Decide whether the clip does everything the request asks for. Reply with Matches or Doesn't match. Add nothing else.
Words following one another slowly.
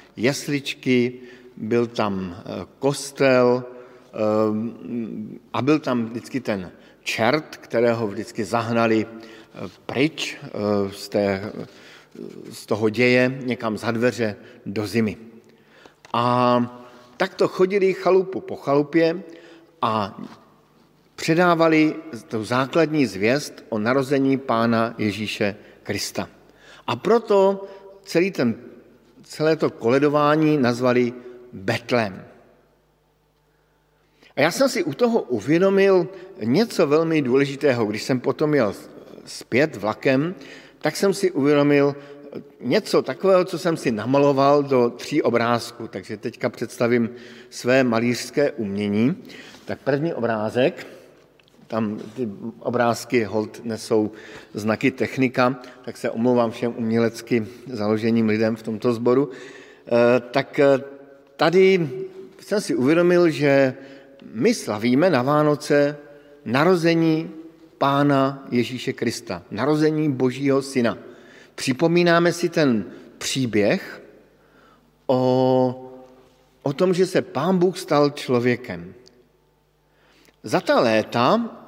Matches